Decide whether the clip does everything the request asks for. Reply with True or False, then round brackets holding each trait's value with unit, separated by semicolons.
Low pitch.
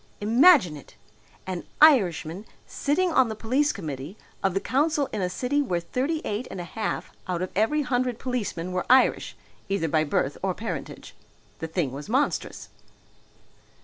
False (215 Hz)